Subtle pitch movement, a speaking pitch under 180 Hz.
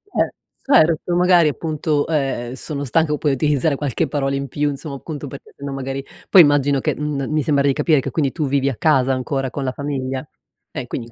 Yes: narrow, 2.2 semitones; medium, 140 Hz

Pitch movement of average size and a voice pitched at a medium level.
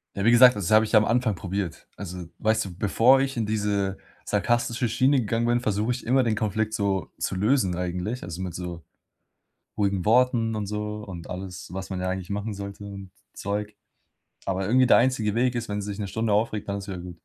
No: average, 3.1 semitones; low, 105 Hz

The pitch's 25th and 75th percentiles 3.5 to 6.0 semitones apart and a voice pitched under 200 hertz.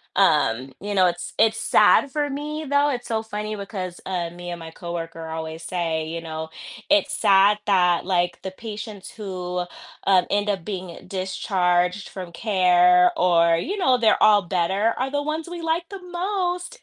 Yes: average, 5.2 semitones; high, 190 Hz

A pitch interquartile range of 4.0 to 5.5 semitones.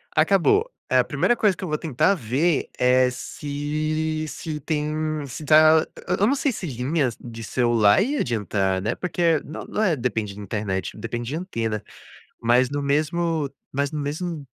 Yes: average, 5.1 semitones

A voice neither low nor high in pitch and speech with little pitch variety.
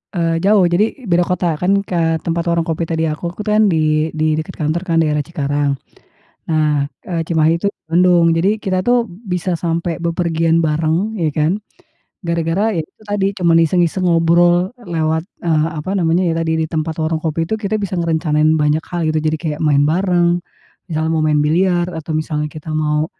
Yes: medium, 165 Hz; narrow, 2.0 semitones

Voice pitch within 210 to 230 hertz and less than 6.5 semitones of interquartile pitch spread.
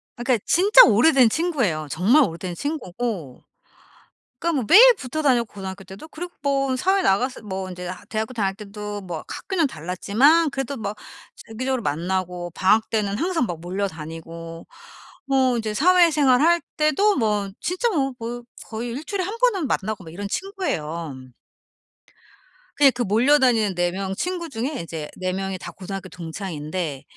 No: high, 220 Hz; wide, 7.6 semitones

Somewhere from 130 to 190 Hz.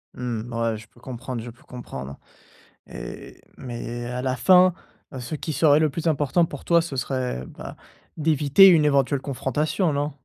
Yes: low, 135 Hz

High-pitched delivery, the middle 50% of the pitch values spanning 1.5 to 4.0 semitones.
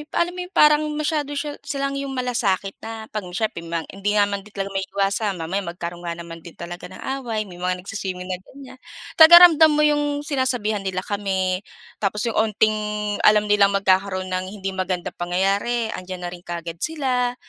No: high, 200 Hz; wide, 5.5 semitones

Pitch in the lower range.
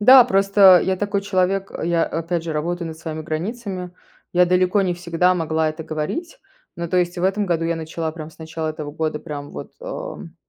No: medium, 175 Hz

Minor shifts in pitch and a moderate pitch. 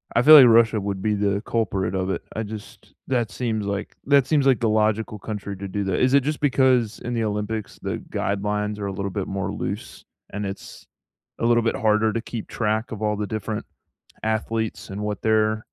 No: narrow, 2.2 semitones; low, 110 Hz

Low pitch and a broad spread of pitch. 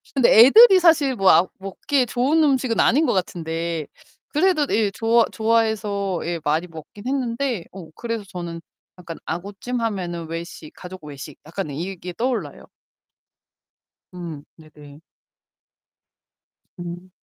No: high, 195 Hz; wide, 6.3 semitones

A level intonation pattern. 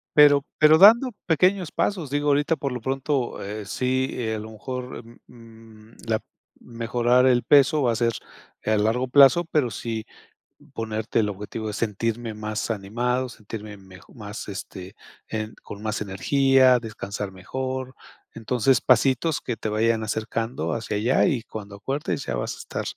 No: average, 3.6 semitones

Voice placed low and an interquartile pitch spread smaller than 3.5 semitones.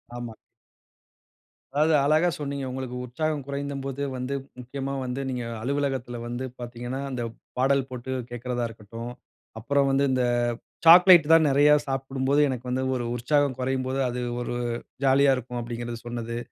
Yes: low, 130 Hz; narrow, 2.5 semitones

